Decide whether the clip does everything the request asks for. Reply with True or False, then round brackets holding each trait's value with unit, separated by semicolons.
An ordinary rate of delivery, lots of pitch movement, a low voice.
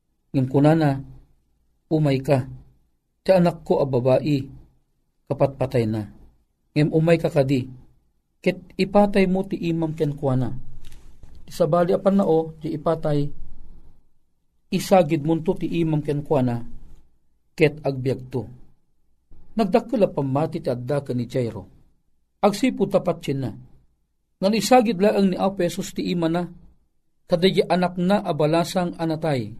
False (130 wpm; 5.9 semitones; 150 Hz)